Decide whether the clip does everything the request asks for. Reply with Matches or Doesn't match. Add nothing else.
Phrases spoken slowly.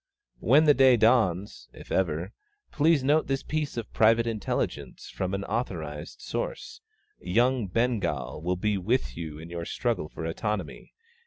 Doesn't match